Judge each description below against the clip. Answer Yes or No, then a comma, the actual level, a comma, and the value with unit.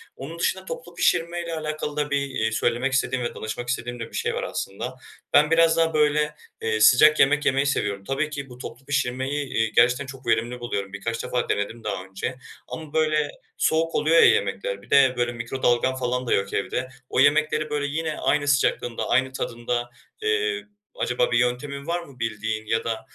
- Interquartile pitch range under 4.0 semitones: No, average, 4.3 semitones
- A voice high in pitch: No, low, 130 Hz